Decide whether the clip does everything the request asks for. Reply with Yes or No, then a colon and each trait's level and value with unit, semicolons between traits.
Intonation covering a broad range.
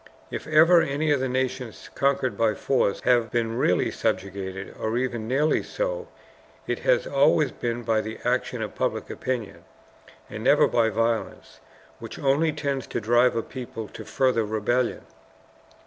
No: average, 3.5 semitones